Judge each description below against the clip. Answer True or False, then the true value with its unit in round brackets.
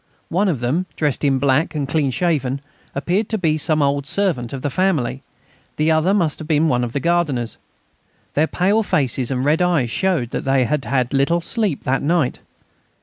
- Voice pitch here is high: False (150 Hz)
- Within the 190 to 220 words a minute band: True (195 wpm)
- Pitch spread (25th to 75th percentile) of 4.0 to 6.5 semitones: True (4.4 semitones)